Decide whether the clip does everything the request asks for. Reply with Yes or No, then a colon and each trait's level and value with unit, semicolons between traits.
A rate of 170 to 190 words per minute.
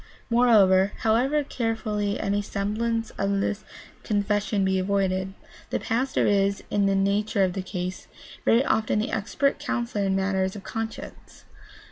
No: average, 140 wpm